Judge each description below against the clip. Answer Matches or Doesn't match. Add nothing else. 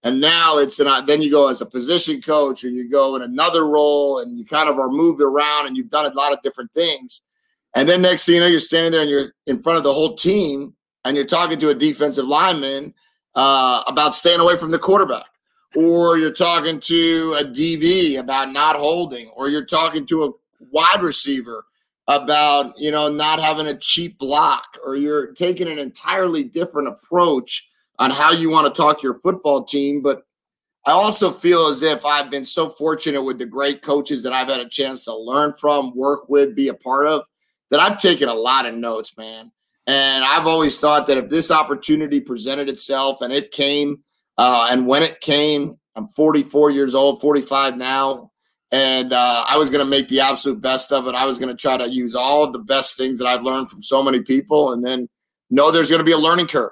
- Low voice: Doesn't match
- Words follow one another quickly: Matches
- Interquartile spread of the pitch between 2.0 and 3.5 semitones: Matches